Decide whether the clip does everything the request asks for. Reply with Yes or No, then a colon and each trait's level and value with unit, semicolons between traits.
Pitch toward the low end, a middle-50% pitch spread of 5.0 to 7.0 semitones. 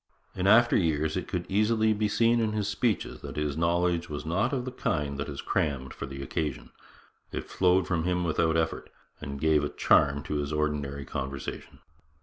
Yes: very low, 80 Hz; average, 5.3 semitones